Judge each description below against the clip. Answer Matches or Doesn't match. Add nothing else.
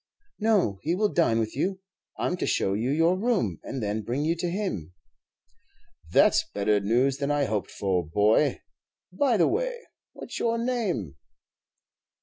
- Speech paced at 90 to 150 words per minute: Doesn't match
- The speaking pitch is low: Doesn't match